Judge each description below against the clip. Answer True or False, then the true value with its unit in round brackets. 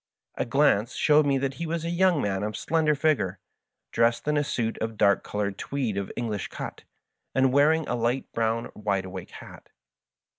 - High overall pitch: False (120 Hz)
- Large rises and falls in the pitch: True (6.0 semitones)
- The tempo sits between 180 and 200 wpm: True (185 wpm)